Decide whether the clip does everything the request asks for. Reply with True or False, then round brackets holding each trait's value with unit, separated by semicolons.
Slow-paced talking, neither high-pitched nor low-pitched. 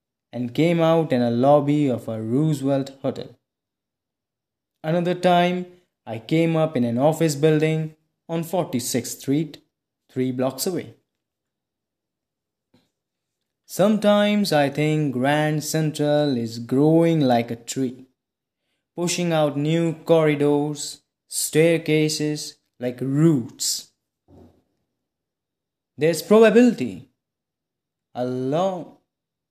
True (95 wpm; 150 Hz)